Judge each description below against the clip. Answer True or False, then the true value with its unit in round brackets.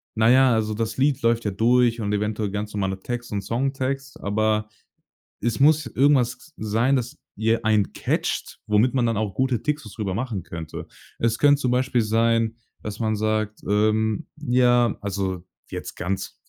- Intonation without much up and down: False (3.1 semitones)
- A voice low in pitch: True (115 Hz)